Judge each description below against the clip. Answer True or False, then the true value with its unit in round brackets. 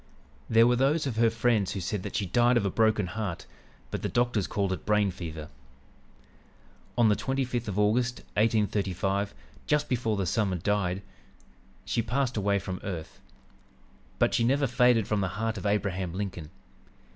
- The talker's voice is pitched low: True (105 Hz)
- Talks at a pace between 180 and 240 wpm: False (170 wpm)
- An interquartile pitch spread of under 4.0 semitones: True (3.6 semitones)